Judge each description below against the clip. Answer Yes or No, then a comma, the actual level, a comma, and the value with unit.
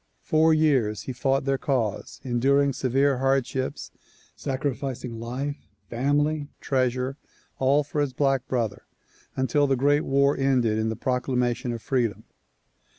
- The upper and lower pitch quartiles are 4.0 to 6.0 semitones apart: No, narrow, 2.4 semitones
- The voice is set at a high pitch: No, low, 135 Hz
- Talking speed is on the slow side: Yes, slow, 130 wpm